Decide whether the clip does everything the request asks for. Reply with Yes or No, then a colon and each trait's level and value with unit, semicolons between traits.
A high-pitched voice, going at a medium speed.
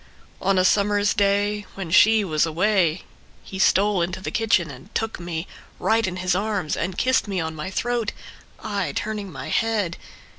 Yes: high, 195 Hz; average, 175 wpm